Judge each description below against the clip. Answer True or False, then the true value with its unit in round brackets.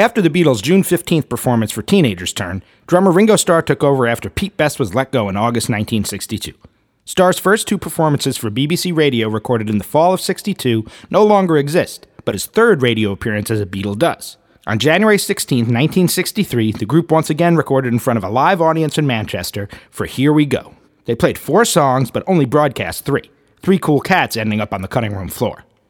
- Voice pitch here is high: False (135 Hz)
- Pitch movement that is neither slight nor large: False (7.8 semitones)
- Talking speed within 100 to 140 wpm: False (200 wpm)